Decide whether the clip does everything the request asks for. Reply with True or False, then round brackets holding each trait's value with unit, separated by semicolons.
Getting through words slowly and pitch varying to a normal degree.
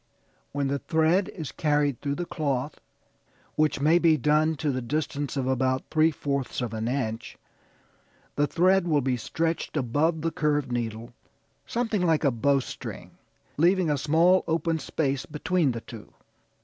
False (155 wpm; 3.5 semitones)